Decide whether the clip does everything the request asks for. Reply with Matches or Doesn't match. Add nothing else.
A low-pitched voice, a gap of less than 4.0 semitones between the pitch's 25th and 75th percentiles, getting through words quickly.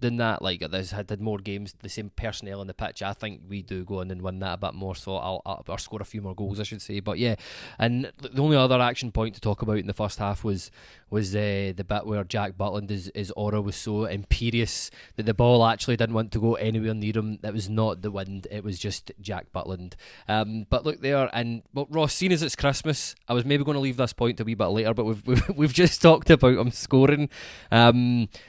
Matches